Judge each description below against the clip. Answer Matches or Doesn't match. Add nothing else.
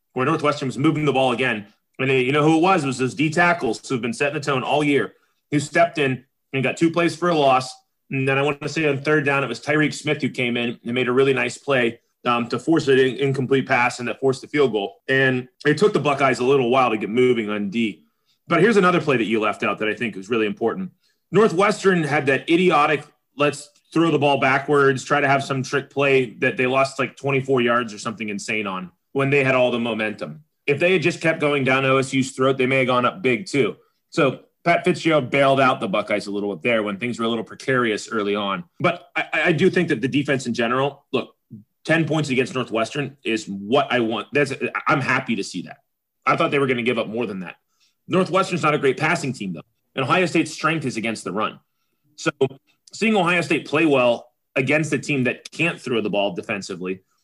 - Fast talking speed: Matches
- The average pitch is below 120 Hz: Doesn't match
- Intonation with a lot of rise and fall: Doesn't match